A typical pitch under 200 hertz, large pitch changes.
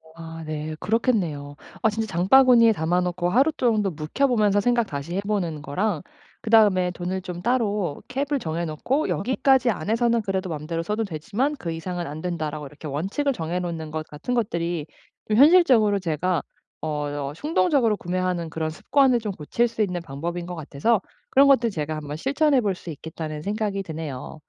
Yes: medium, 185 Hz; wide, 6.1 semitones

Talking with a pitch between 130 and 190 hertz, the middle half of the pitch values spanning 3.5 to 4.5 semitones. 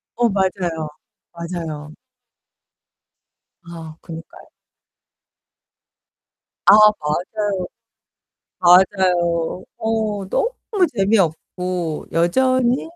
Yes: medium, 185 Hz; average, 4.0 semitones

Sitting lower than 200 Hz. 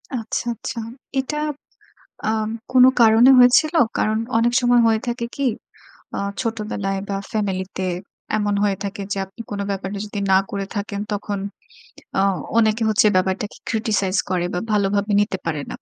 No: high, 210 Hz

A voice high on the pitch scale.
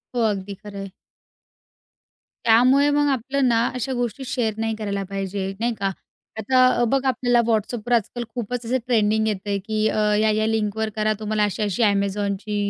Yes: high, 220 Hz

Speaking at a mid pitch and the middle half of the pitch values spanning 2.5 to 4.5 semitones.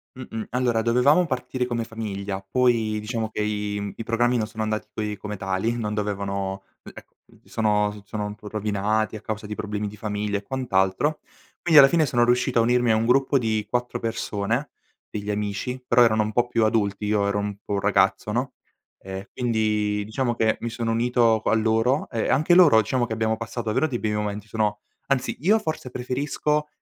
No: low, 110 Hz; average, 2.8 semitones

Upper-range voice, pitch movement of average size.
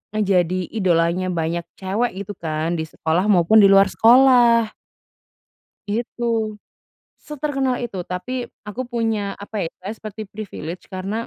Yes: high, 205 Hz; average, 4.2 semitones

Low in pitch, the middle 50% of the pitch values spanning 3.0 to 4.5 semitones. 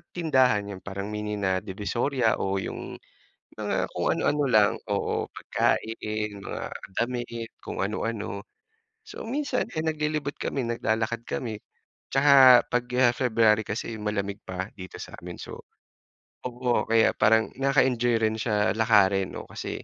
Yes: low, 110 Hz; average, 3.6 semitones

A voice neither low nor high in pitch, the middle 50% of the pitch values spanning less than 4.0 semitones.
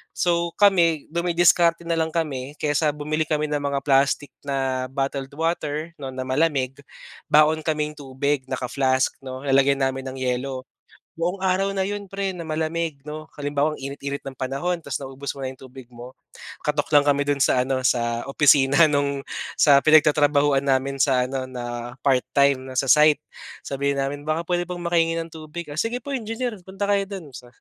Yes: medium, 145 Hz; average, 3.6 semitones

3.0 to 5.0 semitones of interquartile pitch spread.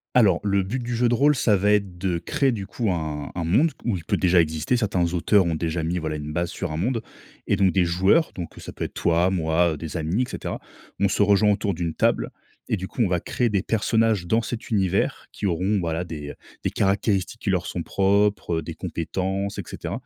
Yes: average, 3.7 semitones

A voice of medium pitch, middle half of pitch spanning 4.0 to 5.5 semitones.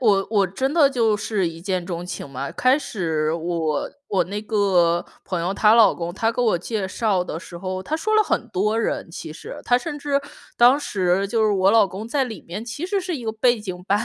No: high, 205 Hz; average, 4.8 semitones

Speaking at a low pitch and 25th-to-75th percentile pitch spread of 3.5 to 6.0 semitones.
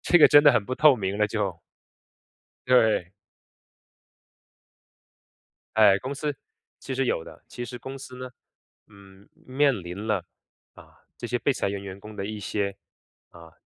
Yes: low, 110 Hz; average, 4.5 semitones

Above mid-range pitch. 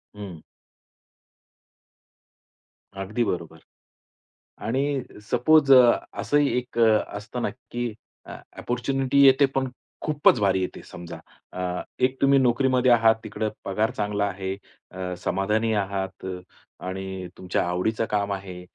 No: low, 110 Hz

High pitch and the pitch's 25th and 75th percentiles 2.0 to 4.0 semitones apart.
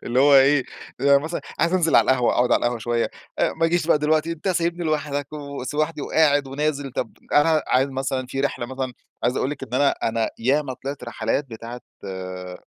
No: medium, 140 Hz; average, 3.6 semitones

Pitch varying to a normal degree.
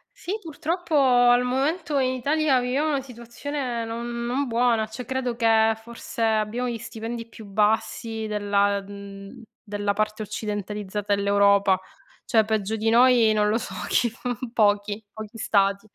Yes: average, 3.0 semitones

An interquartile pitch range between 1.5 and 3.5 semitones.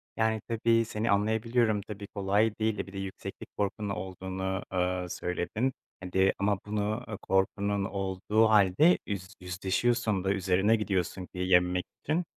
Yes: average, 2.7 semitones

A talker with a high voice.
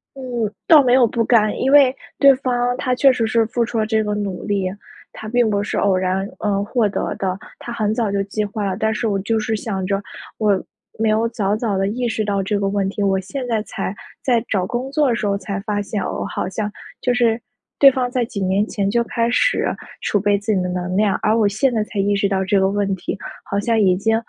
Yes: high, 215 Hz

